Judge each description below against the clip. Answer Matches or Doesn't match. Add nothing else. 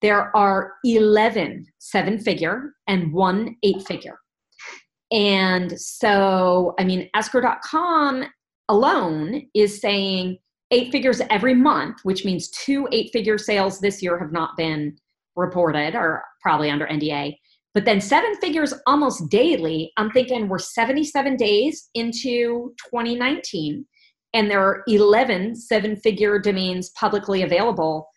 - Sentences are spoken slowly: Matches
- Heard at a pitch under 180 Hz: Doesn't match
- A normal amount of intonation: Matches